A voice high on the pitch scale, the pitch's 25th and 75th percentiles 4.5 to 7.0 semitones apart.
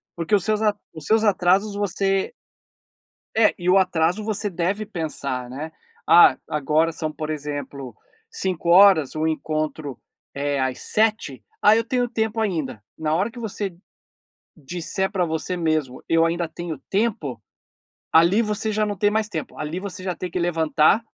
No: medium, 175 Hz; average, 4.8 semitones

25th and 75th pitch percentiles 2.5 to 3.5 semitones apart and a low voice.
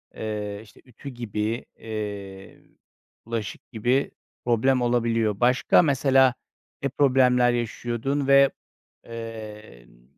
Yes: average, 3.1 semitones; low, 115 Hz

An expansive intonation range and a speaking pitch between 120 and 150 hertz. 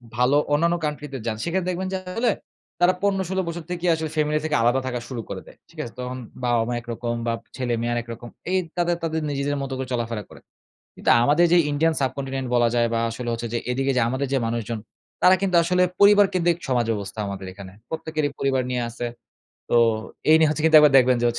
Yes: wide, 5.8 semitones; low, 135 Hz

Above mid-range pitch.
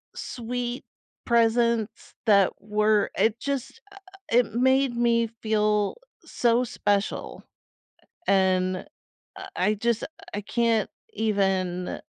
Yes: high, 220 Hz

